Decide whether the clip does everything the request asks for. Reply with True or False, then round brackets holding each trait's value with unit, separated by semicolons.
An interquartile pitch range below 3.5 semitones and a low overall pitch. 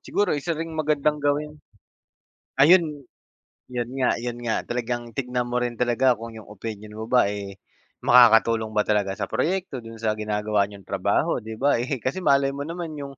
False (4.7 semitones; 120 Hz)